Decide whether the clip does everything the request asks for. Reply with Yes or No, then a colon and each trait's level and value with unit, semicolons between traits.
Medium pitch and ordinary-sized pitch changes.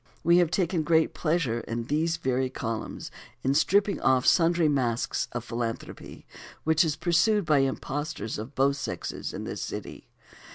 Yes: medium, 150 Hz; average, 4.8 semitones